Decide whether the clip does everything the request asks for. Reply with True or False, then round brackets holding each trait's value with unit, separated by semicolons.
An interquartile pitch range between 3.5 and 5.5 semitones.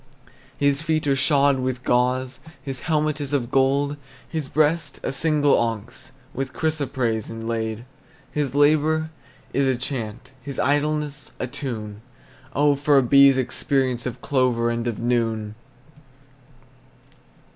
False (3.1 semitones)